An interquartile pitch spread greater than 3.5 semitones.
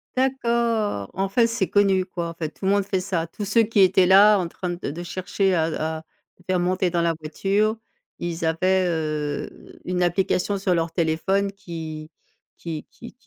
No: average, 3.2 semitones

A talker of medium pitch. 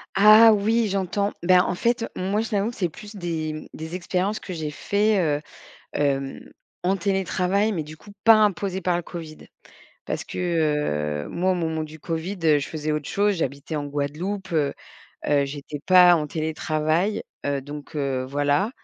Yes: medium, 175 Hz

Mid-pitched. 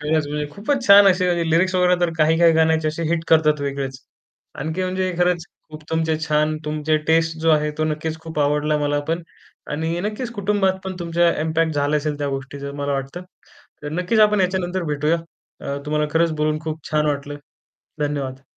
Yes: medium, 160 Hz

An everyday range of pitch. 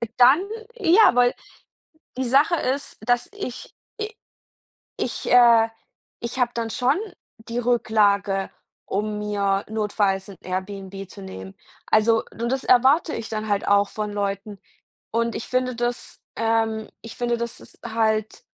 Yes: average, 3.2 semitones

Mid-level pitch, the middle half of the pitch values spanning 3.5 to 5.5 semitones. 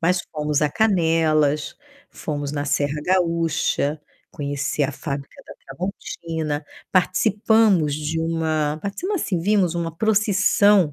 Yes: medium, 165 Hz; average, 4.1 semitones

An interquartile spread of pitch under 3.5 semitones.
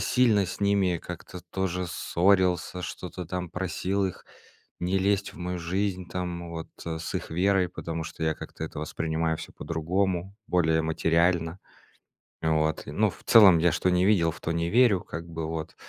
Yes: narrow, 2.4 semitones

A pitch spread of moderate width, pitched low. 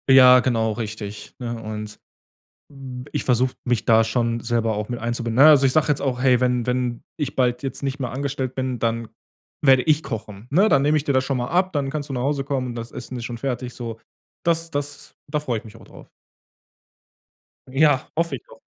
Yes: average, 3.0 semitones; low, 125 Hz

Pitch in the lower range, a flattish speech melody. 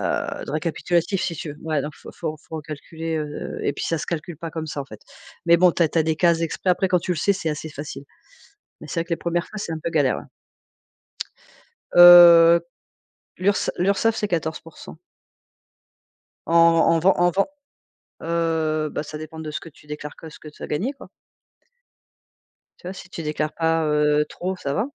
No: medium, 165 Hz; narrow, 2.2 semitones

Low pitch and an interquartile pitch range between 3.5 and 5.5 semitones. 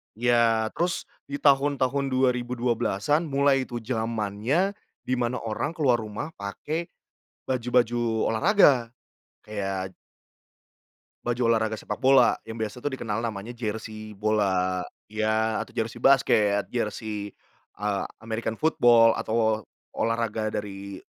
No: low, 115 Hz; average, 3.1 semitones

